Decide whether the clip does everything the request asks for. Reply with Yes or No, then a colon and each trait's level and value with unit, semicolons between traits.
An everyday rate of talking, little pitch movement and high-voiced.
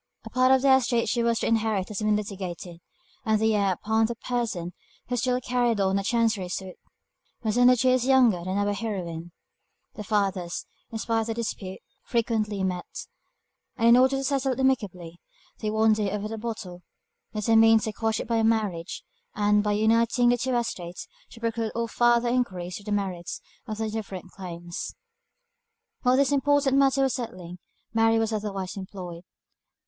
No: average, 180 wpm; average, 3.6 semitones; high, 220 Hz